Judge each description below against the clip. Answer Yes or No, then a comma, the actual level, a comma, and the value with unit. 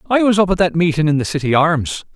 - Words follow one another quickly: Yes, fast, 280 wpm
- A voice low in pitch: No, medium, 165 Hz